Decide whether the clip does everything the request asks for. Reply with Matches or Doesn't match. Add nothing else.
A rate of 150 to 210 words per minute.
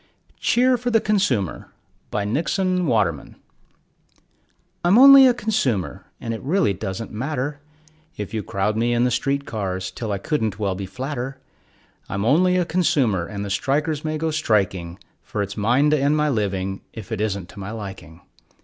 Matches